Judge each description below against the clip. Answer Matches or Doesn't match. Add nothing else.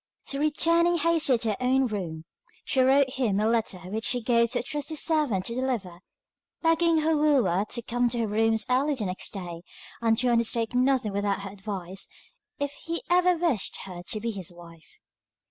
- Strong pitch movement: Matches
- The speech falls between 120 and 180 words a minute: Doesn't match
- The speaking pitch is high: Matches